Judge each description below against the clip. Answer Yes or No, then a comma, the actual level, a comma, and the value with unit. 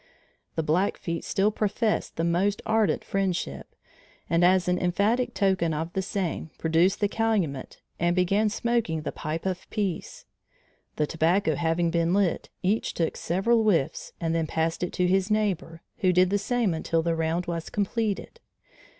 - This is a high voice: No, medium, 180 Hz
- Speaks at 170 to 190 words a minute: No, average, 160 wpm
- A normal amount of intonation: Yes, average, 3.5 semitones